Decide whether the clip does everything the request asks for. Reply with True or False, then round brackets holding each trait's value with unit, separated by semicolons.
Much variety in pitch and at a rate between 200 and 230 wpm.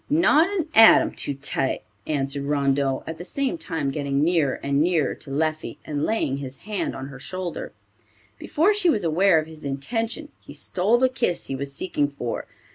False (7.8 semitones; 185 wpm)